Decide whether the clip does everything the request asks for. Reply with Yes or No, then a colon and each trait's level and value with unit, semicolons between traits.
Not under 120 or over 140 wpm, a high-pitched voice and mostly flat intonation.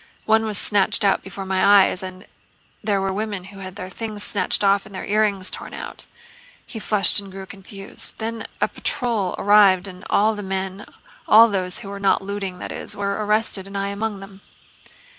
No: average, 185 wpm; high, 200 Hz; narrow, 1.6 semitones